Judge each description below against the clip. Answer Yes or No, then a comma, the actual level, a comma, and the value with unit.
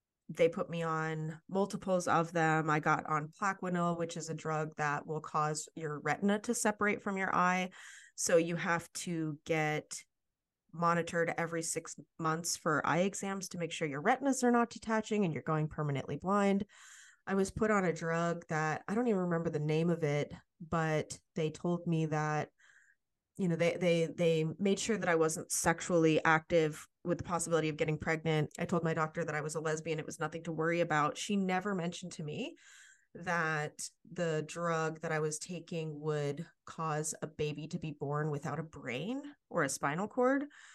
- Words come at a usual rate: Yes, average, 190 wpm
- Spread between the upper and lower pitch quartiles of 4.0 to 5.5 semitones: No, average, 2.8 semitones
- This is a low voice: No, medium, 165 Hz